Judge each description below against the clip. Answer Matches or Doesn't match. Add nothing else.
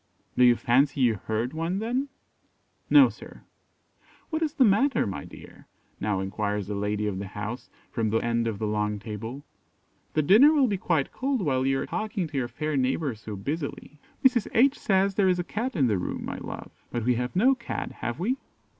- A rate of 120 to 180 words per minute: Doesn't match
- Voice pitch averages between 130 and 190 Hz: Matches